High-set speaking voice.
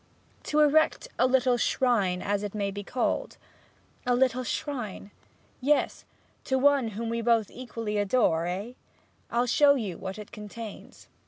Yes: high, 235 Hz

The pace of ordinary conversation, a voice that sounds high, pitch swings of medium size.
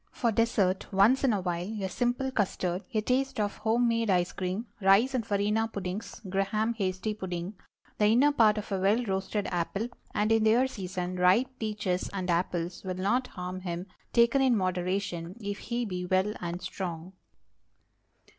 Yes: average, 170 wpm; high, 200 Hz; average, 3.6 semitones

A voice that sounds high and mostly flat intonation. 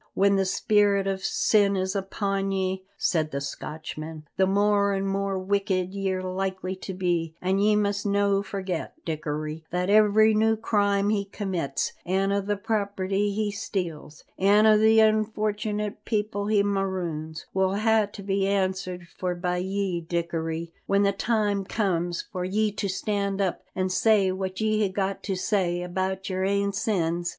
Yes: high, 195 Hz; narrow, 1.8 semitones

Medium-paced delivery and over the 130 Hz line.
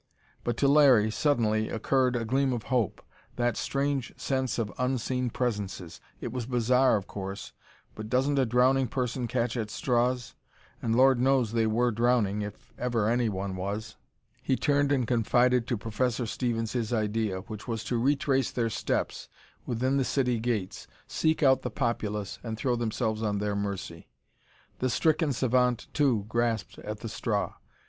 No: average, 160 wpm; low, 120 Hz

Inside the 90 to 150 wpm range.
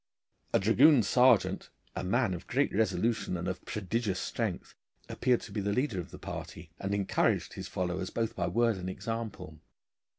No: average, 170 wpm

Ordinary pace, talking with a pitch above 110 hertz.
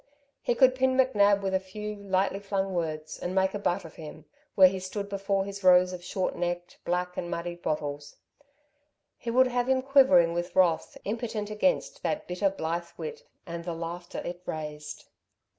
Yes: average, 180 wpm; high, 190 Hz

